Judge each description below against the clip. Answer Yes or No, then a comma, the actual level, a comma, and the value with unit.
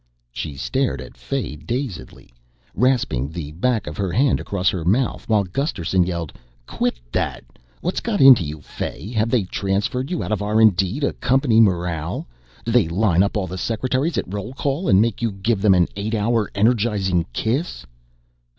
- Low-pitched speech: Yes, low, 105 Hz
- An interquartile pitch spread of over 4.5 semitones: Yes, average, 5.3 semitones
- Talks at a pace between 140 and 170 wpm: No, average, 180 wpm